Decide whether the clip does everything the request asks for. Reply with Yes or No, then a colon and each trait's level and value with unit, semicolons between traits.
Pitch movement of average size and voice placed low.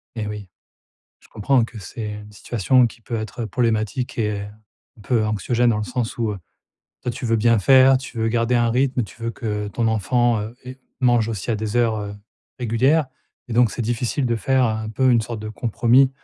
No: narrow, 2.3 semitones; low, 115 Hz